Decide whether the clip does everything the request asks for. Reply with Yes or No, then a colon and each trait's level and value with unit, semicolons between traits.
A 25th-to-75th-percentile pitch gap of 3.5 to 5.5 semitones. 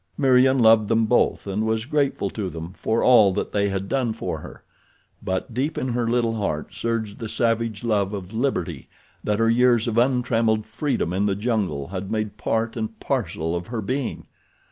No: average, 3.0 semitones